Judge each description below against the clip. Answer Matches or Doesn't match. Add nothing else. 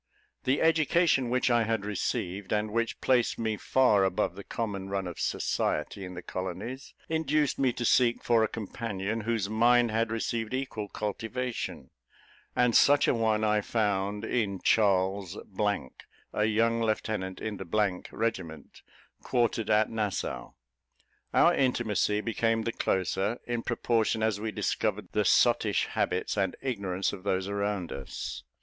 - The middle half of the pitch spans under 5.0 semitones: Matches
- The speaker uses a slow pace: Doesn't match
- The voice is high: Doesn't match